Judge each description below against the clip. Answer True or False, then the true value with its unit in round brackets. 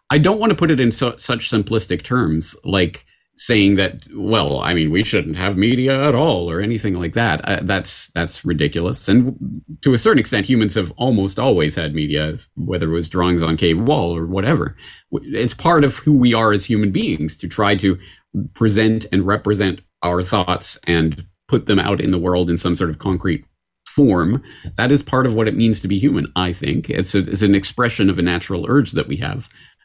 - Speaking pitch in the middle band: False (100 Hz)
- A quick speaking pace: True (210 wpm)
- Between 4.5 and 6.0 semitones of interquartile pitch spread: True (5.2 semitones)